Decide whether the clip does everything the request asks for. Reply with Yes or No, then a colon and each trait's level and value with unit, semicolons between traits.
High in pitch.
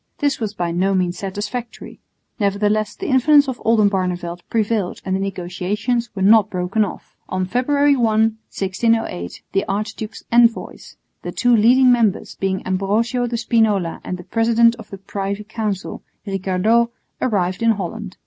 Yes: high, 210 Hz